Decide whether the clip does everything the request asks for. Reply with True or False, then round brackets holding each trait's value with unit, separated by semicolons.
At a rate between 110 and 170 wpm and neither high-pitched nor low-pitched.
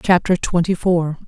True (140 wpm; 175 Hz)